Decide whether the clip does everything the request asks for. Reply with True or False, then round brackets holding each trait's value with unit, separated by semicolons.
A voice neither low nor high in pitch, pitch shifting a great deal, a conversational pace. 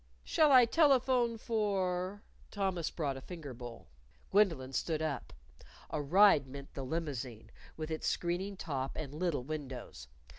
True (160 Hz; 6.5 semitones; 145 wpm)